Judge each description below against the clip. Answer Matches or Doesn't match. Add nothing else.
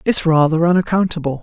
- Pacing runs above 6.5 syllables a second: Doesn't match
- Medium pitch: Matches